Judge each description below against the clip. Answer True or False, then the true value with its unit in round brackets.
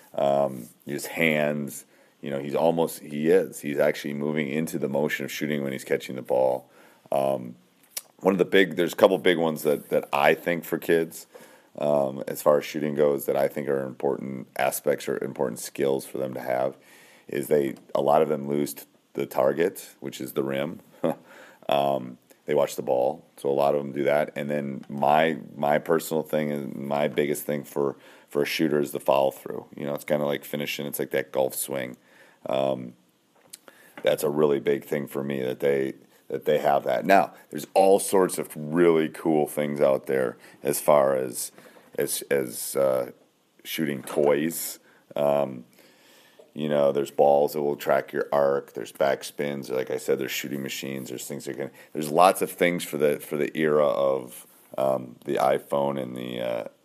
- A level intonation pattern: True (2.0 semitones)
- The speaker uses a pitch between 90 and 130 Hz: False (70 Hz)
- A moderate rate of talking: True (190 wpm)